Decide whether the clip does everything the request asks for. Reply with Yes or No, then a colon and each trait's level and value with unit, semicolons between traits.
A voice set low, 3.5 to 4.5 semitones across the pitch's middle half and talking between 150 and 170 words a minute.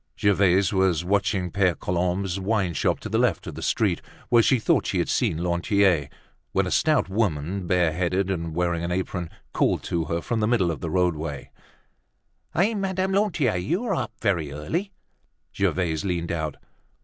Yes: very low, 90 Hz; average, 4.0 semitones; average, 165 wpm